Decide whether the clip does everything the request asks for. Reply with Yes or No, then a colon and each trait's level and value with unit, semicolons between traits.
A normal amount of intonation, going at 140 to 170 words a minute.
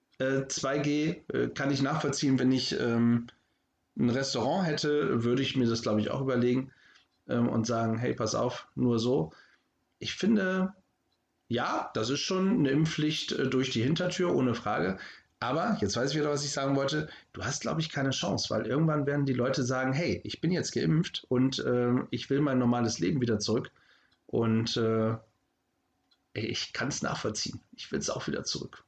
No: average, 3.8 semitones; average, 180 wpm